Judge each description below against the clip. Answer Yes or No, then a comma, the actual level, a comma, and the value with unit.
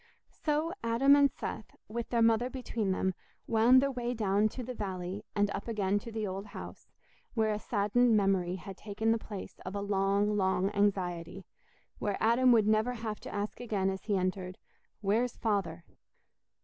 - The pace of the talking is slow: No, average, 175 wpm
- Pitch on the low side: No, high, 210 Hz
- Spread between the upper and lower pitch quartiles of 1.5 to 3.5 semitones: Yes, average, 3.0 semitones